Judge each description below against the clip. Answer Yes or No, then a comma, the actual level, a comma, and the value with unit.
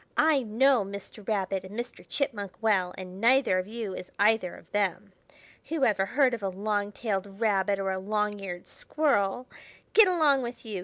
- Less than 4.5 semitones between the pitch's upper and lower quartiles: Yes, average, 3.8 semitones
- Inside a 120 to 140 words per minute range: No, average, 185 wpm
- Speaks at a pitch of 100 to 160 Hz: No, high, 210 Hz